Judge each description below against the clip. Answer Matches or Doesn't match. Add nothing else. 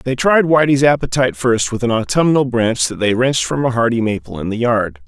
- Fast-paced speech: Matches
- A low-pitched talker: Matches